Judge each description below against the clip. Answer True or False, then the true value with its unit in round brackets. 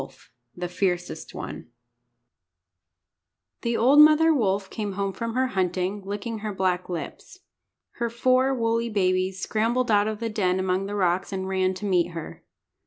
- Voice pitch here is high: True (200 Hz)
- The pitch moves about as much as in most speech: True (3.8 semitones)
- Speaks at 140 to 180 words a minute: True (160 wpm)